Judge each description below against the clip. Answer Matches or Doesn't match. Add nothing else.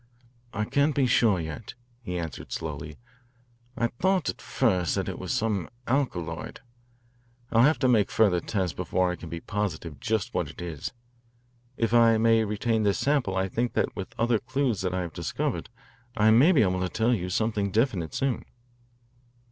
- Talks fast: Doesn't match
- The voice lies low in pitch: Matches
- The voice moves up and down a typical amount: Matches